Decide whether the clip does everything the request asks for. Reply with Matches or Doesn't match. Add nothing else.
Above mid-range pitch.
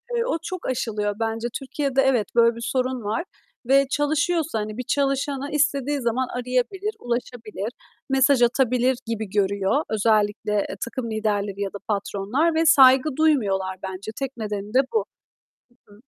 Matches